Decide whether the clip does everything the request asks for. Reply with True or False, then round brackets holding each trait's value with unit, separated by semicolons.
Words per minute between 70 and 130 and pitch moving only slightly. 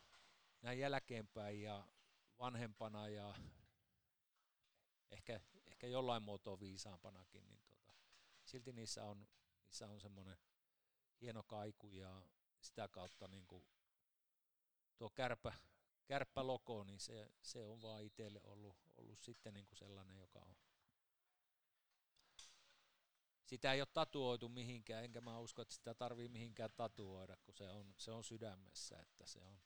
False (125 wpm; 3.2 semitones)